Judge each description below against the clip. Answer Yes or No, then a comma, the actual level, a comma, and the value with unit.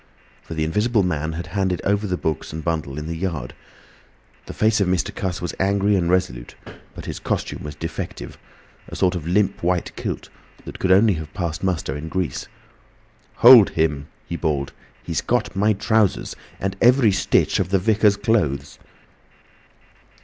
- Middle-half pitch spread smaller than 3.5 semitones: No, average, 3.9 semitones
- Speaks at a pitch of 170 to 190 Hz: No, very low, 90 Hz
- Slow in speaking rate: No, average, 170 wpm